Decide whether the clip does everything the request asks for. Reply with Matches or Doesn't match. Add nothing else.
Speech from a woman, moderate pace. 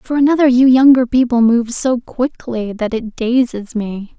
Matches